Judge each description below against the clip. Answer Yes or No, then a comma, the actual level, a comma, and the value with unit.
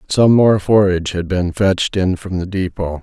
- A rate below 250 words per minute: Yes, average, 200 wpm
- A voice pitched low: Yes, very low, 95 Hz